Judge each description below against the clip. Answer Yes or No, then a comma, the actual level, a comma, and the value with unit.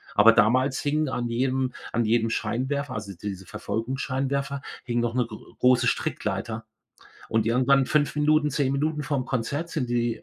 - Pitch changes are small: No, average, 3.2 semitones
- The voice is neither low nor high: No, low, 130 Hz